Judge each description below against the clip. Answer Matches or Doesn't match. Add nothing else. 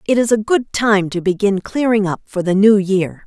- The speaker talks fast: Matches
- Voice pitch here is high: Matches